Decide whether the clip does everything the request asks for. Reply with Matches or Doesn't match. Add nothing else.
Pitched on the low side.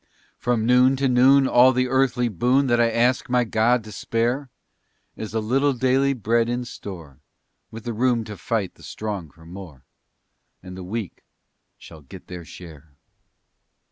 Matches